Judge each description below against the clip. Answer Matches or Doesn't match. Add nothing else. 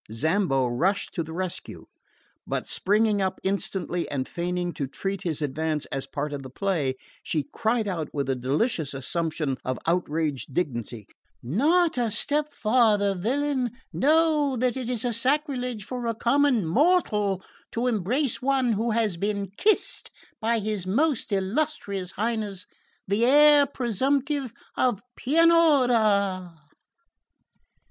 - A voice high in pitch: Matches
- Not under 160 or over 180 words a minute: Doesn't match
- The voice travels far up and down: Matches